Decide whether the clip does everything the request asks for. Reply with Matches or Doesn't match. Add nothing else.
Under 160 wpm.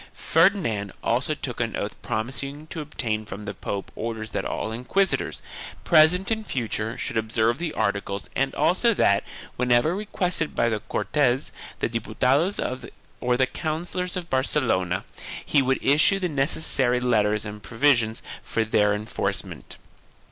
Matches